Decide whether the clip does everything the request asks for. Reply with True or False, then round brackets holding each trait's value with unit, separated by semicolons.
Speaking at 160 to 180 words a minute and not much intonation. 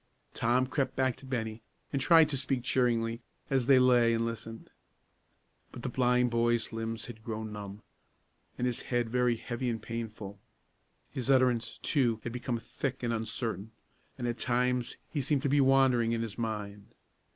True (170 wpm; 2.1 semitones)